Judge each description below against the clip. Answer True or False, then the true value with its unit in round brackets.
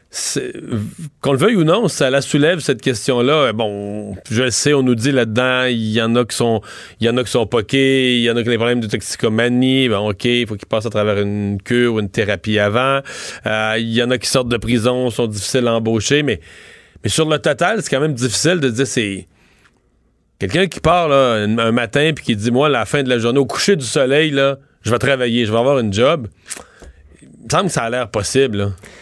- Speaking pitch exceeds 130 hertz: False (120 Hz)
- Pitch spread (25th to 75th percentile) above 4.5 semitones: False (3.5 semitones)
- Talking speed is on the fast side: True (245 wpm)